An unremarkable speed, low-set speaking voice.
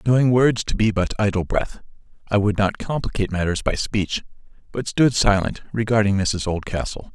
Yes: average, 170 wpm; low, 105 Hz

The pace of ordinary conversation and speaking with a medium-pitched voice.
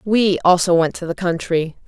Yes: average, 190 wpm; medium, 175 Hz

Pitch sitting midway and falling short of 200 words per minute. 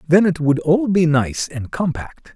No: medium, 160 Hz; fast, 205 wpm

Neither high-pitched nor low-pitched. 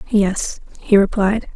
No: high, 200 Hz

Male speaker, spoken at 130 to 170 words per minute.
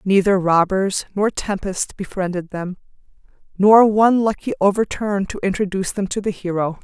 No: female; average, 140 wpm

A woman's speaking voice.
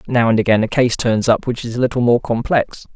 No: male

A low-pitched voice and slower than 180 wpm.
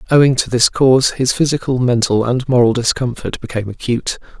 Yes: low, 125 Hz; average, 165 wpm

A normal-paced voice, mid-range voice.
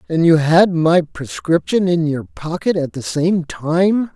Yes: average, 175 wpm; medium, 160 Hz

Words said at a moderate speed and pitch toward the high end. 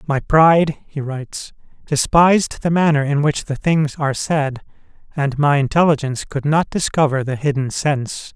No: average, 160 wpm; medium, 145 Hz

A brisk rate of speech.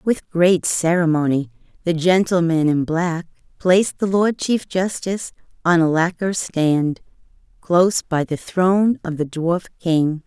No: average, 140 wpm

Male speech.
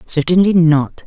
No: female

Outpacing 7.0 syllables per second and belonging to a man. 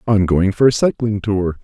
No: 4.7 syllables/s; male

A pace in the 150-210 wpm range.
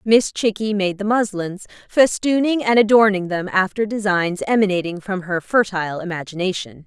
No: average, 140 wpm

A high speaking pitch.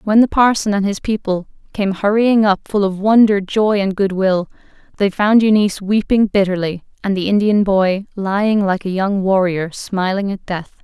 Yes: high, 200 Hz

